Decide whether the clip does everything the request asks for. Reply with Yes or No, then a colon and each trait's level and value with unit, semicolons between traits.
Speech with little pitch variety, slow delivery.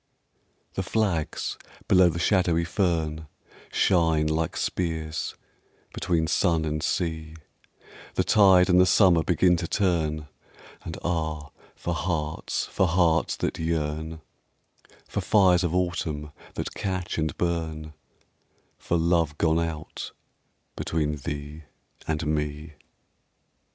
Yes: narrow, 2.2 semitones; slow, 115 wpm